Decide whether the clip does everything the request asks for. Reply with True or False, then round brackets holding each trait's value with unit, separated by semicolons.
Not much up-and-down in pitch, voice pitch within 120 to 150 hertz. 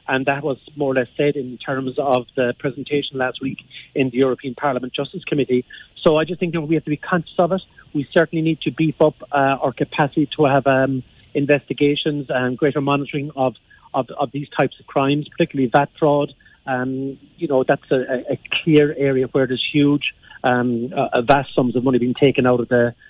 True (2.3 semitones; 140 Hz)